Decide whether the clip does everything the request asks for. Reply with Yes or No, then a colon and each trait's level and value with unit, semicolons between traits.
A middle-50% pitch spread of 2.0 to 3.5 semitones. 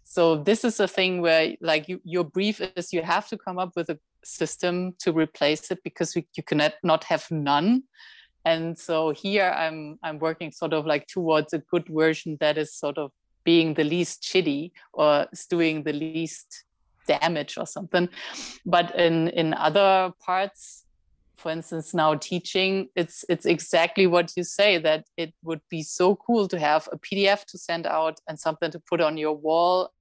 Yes: narrow, 2.6 semitones